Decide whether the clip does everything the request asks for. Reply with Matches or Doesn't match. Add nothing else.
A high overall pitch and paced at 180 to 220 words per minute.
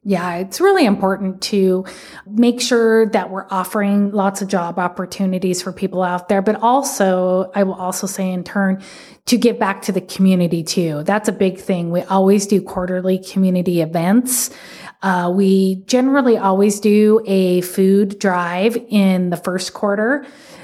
Doesn't match